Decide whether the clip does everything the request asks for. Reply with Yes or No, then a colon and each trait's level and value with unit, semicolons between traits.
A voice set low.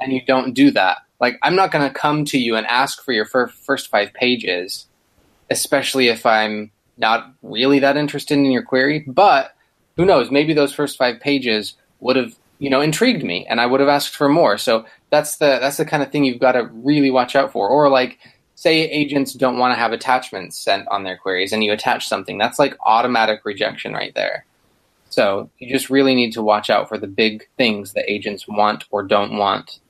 Yes: low, 130 Hz